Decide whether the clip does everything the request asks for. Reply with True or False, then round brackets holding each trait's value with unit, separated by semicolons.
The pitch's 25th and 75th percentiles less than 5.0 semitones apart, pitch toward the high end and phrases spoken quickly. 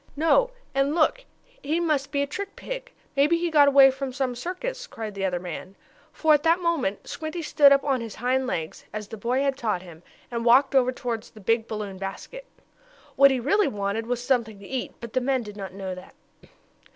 False (5.6 semitones; 260 Hz; 210 wpm)